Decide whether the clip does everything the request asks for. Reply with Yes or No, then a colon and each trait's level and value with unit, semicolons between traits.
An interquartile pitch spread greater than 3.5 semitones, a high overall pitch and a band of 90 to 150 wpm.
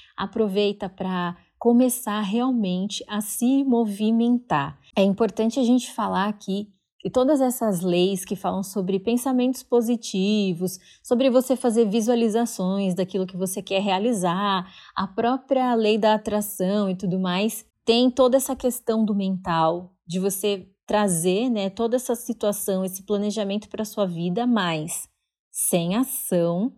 Yes: average, 3.9 semitones; high, 210 Hz; average, 135 wpm